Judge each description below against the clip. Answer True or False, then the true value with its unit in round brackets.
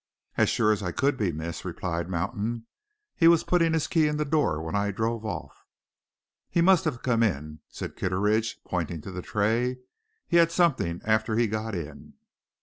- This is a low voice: True (110 Hz)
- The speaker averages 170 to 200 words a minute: True (185 wpm)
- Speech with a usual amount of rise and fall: False (7.5 semitones)